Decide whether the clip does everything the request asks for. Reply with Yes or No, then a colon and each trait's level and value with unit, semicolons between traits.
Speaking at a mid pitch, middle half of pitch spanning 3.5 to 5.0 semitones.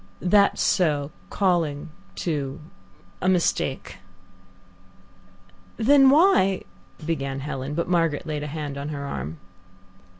Yes: medium, 155 Hz; average, 4.3 semitones